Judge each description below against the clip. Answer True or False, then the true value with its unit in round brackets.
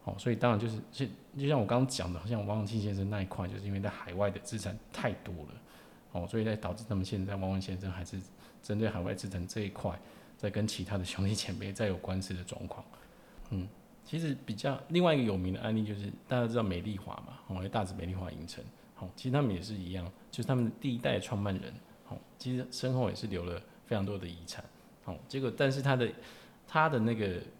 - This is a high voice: False (105 Hz)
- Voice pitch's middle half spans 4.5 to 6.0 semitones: False (4.1 semitones)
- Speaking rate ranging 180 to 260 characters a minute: False (340 characters per minute)